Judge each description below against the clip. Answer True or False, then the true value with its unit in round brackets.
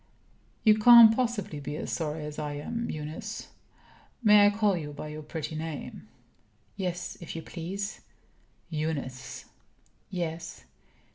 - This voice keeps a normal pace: False (130 wpm)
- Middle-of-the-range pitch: True (165 Hz)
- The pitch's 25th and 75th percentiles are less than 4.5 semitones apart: False (5.2 semitones)